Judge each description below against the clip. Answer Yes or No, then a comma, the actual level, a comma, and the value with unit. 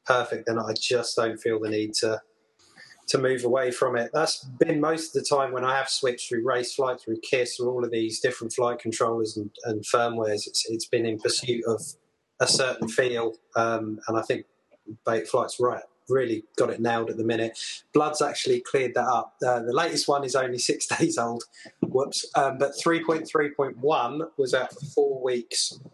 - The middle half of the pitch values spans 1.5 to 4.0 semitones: No, average, 4.9 semitones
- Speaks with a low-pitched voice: Yes, low, 125 Hz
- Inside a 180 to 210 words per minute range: Yes, fast, 205 wpm